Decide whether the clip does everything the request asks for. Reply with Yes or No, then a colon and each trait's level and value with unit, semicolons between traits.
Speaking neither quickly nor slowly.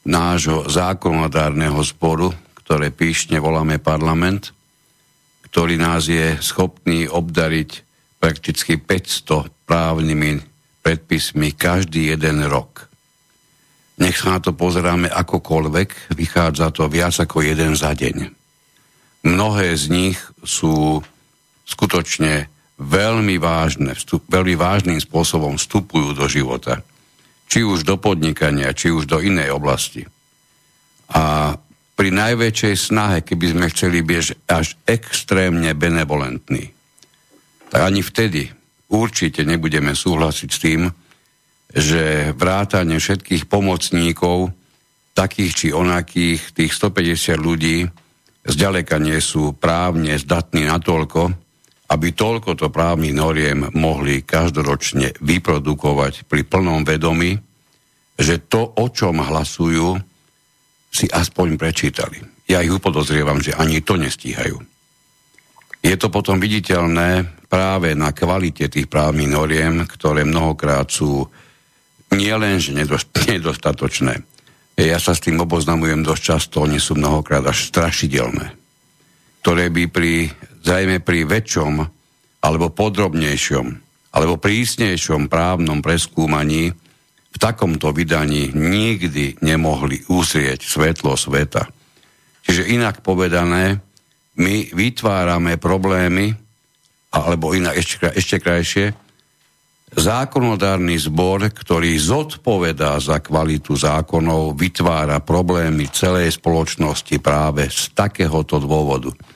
No: slow, 105 wpm